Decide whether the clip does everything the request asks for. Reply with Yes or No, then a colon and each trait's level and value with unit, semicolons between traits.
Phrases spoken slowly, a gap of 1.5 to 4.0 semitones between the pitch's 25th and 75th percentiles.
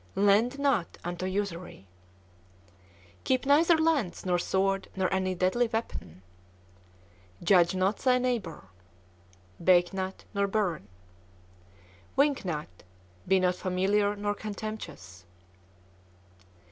Yes: slow, 100 wpm; average, 3.5 semitones